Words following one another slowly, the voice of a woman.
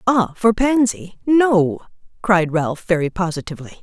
Yes: slow, 125 wpm; female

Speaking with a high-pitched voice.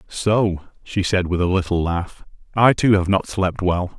No: very low, 95 Hz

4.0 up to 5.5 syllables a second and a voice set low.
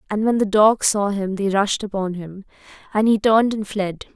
No: 5.0 syllables/s; high, 205 Hz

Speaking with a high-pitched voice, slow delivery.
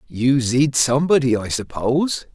No: low, 135 Hz; slow, 130 wpm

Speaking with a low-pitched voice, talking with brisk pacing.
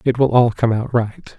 Yes: low, 120 Hz; fast, 260 wpm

